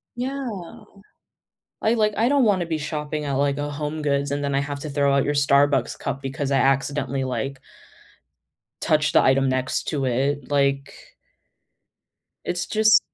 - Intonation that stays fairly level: Yes, narrow, 2.1 semitones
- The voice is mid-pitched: Yes, medium, 145 Hz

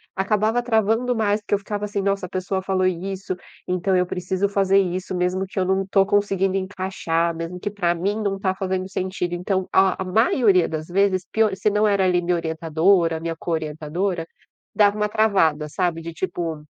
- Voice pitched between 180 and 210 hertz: Yes, high, 190 Hz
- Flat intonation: Yes, narrow, 2.3 semitones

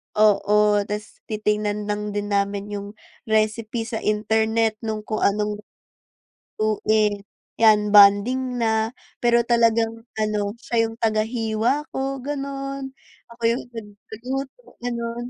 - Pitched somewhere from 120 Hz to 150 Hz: No, high, 220 Hz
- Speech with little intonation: Yes, narrow, 2.0 semitones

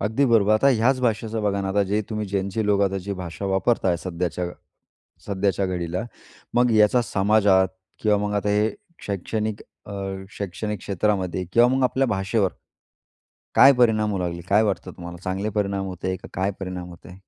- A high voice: No, low, 100 Hz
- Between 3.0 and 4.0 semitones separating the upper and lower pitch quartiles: No, narrow, 2.5 semitones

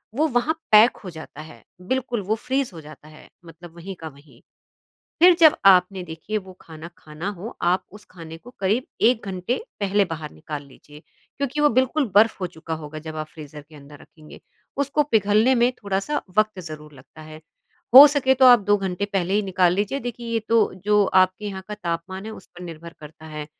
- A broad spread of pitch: Yes, wide, 6.1 semitones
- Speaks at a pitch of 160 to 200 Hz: Yes, high, 190 Hz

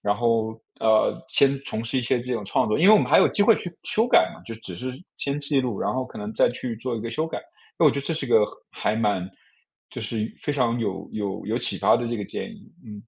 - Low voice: Yes, low, 120 Hz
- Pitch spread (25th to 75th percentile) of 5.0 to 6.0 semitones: No, average, 4.5 semitones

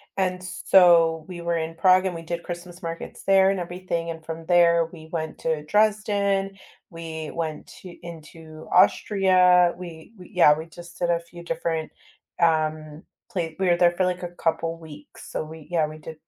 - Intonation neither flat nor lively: No, narrow, 2.1 semitones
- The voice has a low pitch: No, medium, 170 Hz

